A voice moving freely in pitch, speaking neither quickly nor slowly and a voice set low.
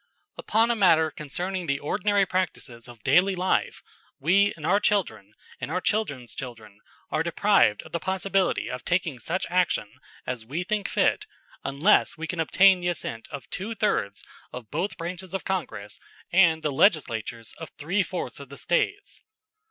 No: wide, 6.7 semitones; average, 160 wpm; medium, 170 Hz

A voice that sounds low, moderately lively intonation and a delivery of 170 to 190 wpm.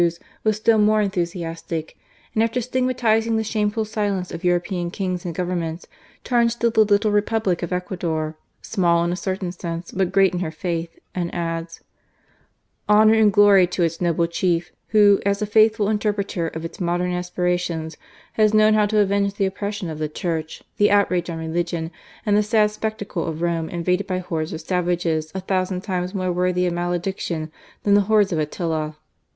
No: medium, 180 Hz; average, 3.5 semitones; average, 180 wpm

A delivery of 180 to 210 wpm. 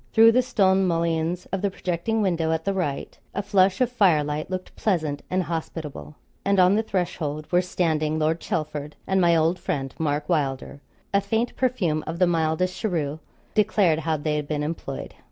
Yes: average, 185 wpm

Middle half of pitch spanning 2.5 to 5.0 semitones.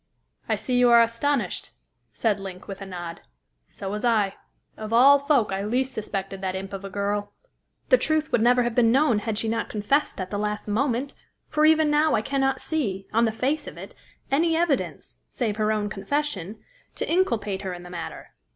No: wide, 5.4 semitones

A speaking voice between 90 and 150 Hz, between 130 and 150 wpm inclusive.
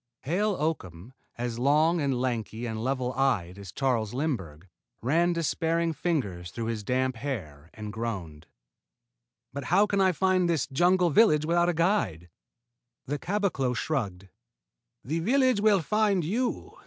Yes: medium, 140 Hz; average, 140 wpm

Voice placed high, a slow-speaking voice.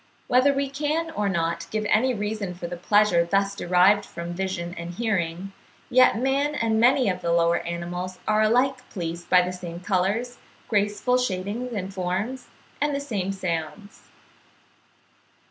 No: high, 200 Hz; average, 155 wpm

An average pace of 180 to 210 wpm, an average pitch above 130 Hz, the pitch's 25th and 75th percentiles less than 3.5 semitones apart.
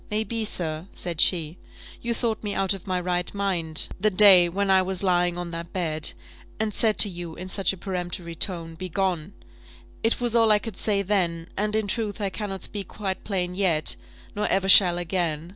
Yes: average, 200 wpm; high, 190 Hz; average, 2.9 semitones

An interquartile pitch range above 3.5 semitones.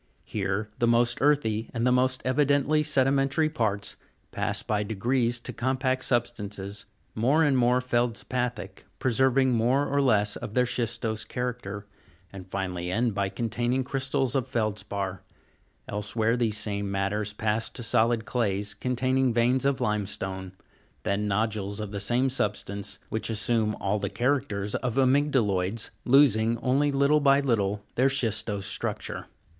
Yes: average, 3.9 semitones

